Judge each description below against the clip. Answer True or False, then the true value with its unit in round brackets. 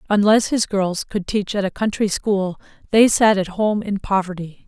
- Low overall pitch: False (200 Hz)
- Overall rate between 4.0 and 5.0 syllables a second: True (4.4 syllables/s)